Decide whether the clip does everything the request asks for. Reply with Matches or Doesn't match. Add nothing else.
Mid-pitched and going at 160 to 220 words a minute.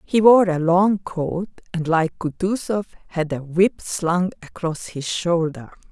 Doesn't match